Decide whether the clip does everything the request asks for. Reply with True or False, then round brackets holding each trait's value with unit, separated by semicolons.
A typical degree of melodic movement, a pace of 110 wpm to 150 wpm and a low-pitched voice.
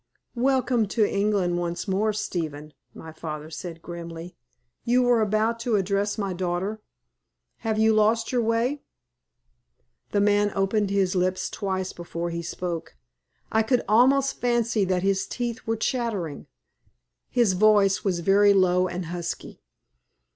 False (3.8 semitones; 140 wpm; 200 Hz)